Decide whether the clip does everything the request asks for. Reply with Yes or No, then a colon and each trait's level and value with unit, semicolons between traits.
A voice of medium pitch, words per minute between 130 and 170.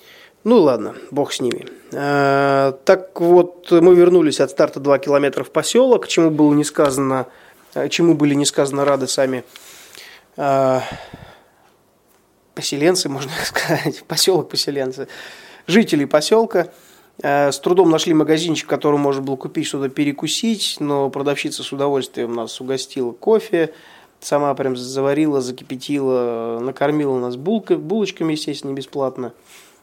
No: medium, 145 Hz; average, 115 wpm